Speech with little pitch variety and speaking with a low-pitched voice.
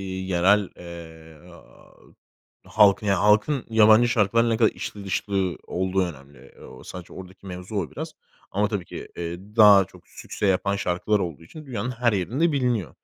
No: average, 3.4 semitones; low, 100 Hz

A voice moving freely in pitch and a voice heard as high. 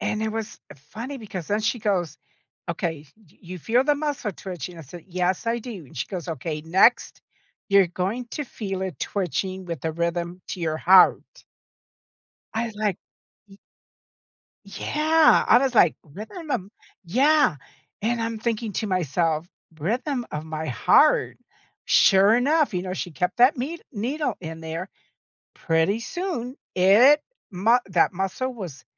Yes: wide, 5.7 semitones; high, 195 Hz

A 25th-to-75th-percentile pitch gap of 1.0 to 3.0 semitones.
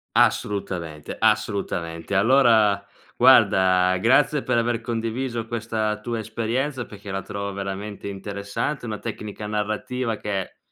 Yes: average, 2.7 semitones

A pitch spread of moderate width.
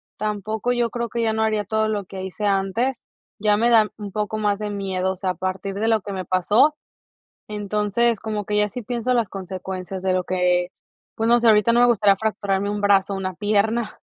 No: narrow, 2.3 semitones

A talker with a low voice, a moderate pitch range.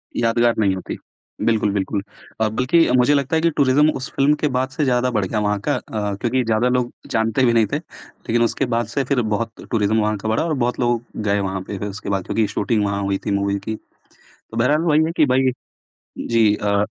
Yes: low, 115 Hz; average, 3.9 semitones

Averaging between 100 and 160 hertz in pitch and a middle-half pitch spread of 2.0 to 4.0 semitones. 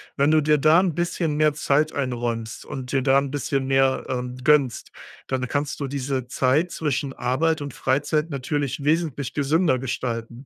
Yes: medium, 140 Hz; average, 2.7 semitones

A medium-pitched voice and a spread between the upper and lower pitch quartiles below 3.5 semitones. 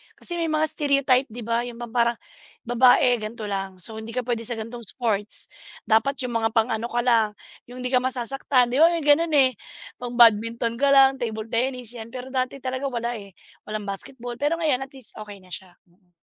No: high, 240 Hz; average, 2.9 semitones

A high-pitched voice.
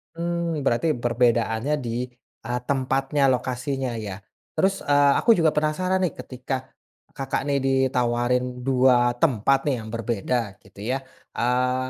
No: low, 130 Hz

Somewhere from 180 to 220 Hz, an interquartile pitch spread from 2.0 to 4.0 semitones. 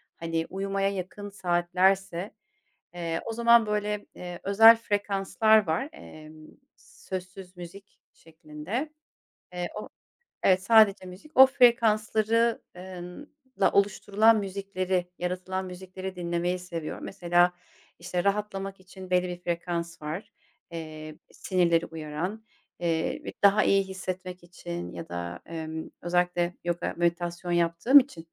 Yes: medium, 185 Hz; narrow, 2.5 semitones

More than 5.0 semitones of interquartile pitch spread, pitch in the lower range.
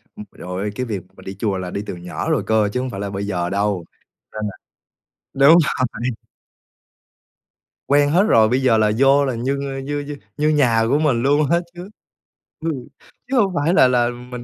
Yes: wide, 5.6 semitones; low, 125 Hz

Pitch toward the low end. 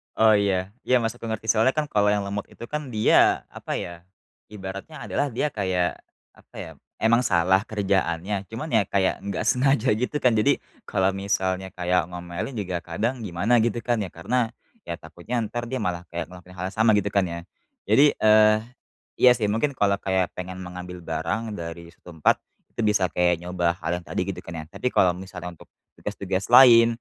Yes: low, 100 Hz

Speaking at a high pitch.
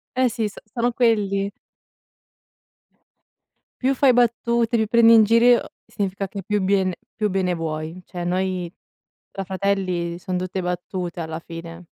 Yes: high, 195 Hz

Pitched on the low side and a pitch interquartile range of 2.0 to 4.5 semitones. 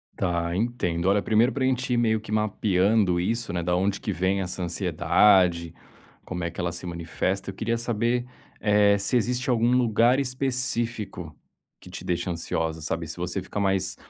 No: low, 100 Hz; average, 4.9 semitones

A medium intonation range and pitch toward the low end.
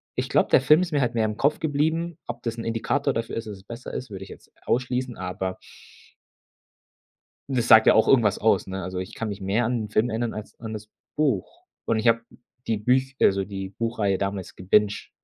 Yes: average, 3.8 semitones; low, 115 Hz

